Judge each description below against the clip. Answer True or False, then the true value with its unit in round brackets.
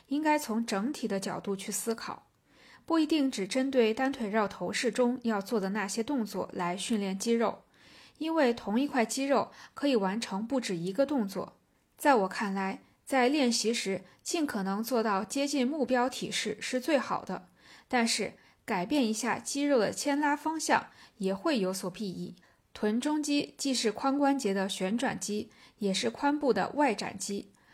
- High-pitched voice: True (230 Hz)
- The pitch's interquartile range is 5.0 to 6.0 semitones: True (5.4 semitones)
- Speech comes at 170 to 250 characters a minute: True (245 characters per minute)